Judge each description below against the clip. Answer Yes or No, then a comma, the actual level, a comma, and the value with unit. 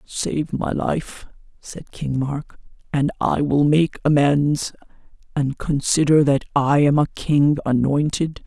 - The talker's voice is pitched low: No, medium, 145 Hz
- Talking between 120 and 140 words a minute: Yes, slow, 135 wpm